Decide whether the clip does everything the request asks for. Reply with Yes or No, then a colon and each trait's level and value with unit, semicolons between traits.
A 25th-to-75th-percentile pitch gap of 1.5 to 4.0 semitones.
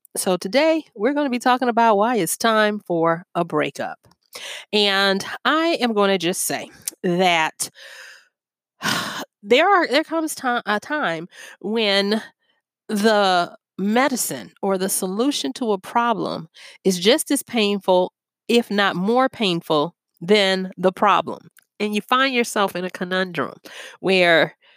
No: average, 4.6 semitones